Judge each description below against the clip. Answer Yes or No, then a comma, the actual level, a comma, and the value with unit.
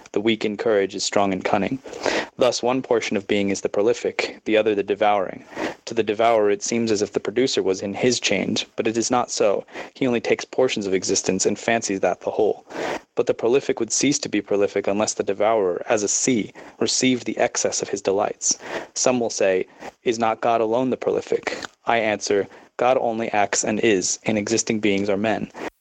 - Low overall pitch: Yes, low, 115 Hz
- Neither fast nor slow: No, fast, 210 wpm